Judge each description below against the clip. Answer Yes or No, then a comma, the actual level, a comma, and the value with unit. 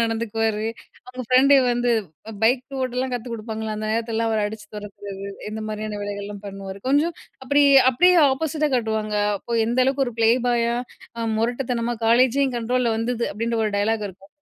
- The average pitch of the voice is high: Yes, high, 230 Hz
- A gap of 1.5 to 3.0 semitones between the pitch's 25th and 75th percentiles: Yes, narrow, 2.6 semitones